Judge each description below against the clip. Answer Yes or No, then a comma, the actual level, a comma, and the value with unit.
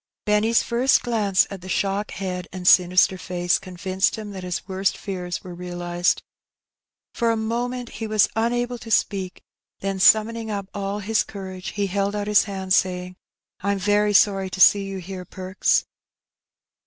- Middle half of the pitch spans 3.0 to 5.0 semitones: No, narrow, 2.4 semitones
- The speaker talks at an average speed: Yes, average, 165 wpm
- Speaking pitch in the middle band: No, high, 195 Hz